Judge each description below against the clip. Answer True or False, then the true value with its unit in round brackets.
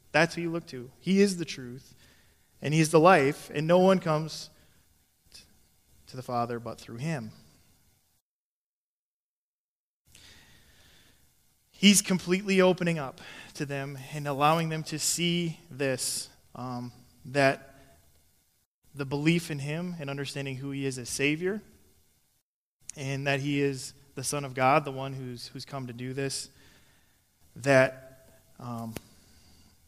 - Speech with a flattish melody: False (4.5 semitones)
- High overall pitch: False (135 Hz)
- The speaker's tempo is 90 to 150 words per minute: True (135 wpm)